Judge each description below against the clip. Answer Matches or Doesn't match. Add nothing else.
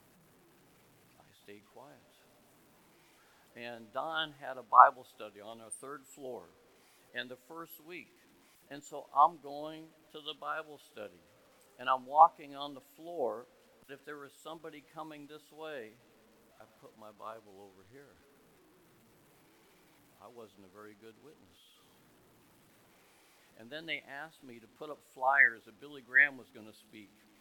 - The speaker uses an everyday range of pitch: Doesn't match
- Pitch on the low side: Matches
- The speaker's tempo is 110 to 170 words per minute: Matches